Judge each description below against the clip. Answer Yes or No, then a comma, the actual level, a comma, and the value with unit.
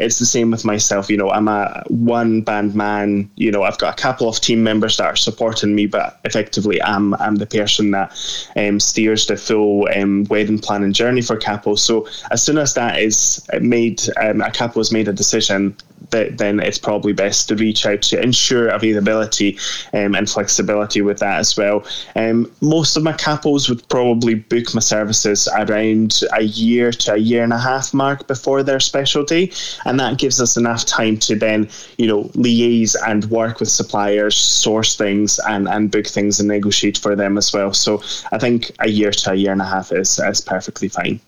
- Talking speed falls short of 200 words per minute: No, fast, 205 wpm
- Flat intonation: Yes, narrow, 2.2 semitones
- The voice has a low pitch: Yes, low, 110 Hz